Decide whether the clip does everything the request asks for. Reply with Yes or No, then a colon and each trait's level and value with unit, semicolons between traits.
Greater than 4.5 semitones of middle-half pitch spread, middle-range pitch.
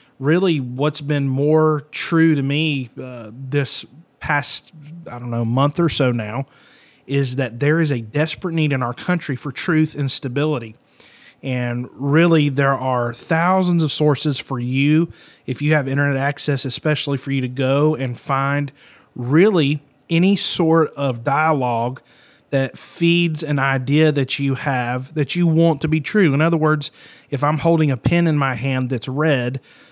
No: average, 2.9 semitones; medium, 145 Hz